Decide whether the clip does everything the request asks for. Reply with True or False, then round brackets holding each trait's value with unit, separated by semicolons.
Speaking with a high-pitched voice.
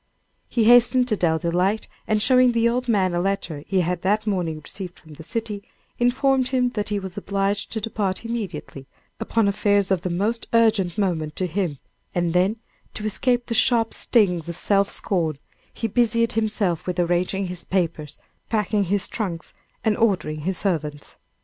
True (200 Hz)